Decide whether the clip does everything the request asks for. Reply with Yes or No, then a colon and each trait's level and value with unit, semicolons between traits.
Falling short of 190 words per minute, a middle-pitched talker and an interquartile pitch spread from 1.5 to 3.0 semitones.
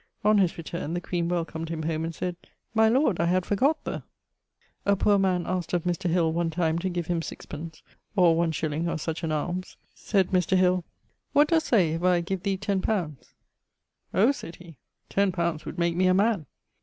No: fast, 205 wpm; medium, 175 Hz; narrow, 2.6 semitones